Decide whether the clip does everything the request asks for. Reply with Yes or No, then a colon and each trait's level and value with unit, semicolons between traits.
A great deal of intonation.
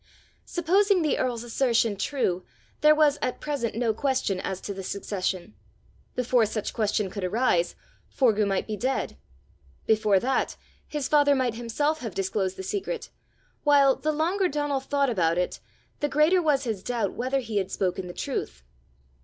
Yes: wide, 6.3 semitones